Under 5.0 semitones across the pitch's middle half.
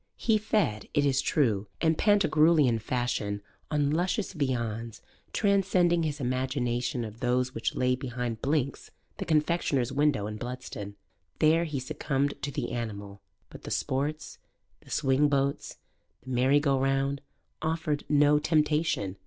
Yes: average, 3.8 semitones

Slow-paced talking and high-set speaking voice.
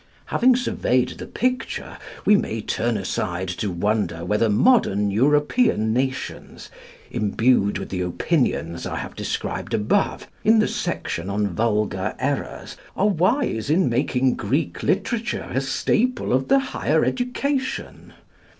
No: slow, 130 wpm; low, 125 Hz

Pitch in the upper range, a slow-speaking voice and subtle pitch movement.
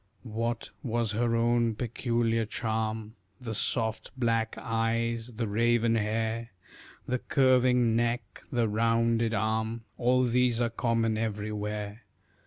No: low, 115 Hz; slow, 115 wpm; narrow, 1.2 semitones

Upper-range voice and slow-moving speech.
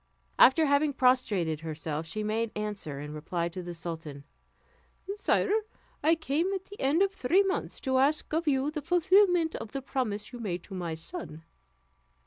No: very high, 250 Hz; average, 170 wpm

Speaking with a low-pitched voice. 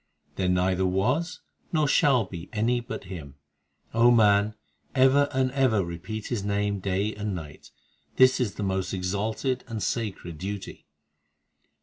Yes: low, 105 Hz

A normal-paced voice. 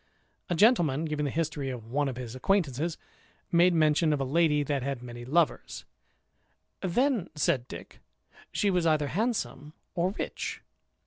Yes: average, 150 wpm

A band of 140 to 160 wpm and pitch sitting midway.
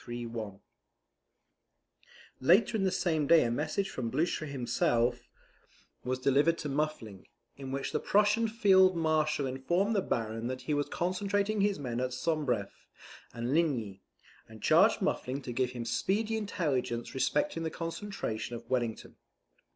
Yes: average, 145 wpm; medium, 145 Hz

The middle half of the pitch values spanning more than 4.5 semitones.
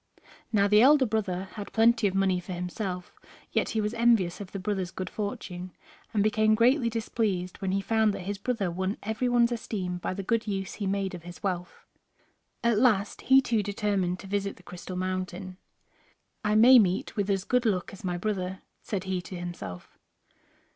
No: average, 3.1 semitones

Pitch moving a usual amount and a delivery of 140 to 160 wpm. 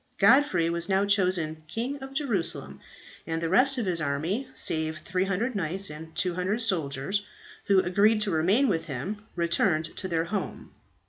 Yes: average, 4.4 semitones; average, 155 wpm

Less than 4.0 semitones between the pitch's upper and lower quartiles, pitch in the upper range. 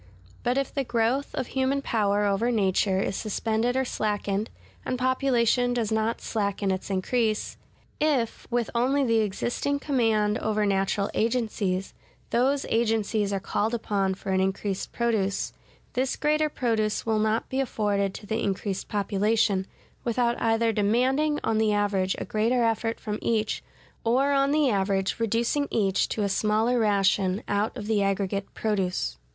Yes: average, 3.3 semitones; high, 220 Hz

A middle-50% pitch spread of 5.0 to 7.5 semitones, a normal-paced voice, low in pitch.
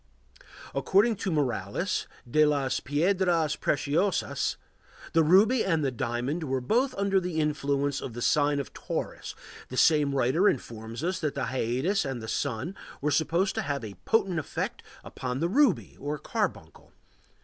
No: average, 5.3 semitones; average, 155 wpm; medium, 150 Hz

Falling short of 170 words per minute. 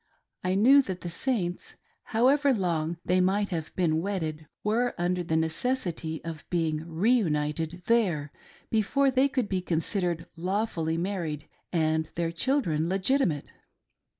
Yes: slow, 135 wpm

